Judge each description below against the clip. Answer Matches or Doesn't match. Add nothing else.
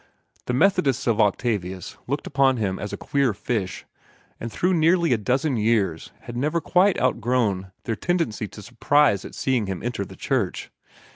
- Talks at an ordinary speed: Matches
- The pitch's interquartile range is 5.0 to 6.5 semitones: Matches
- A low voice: Matches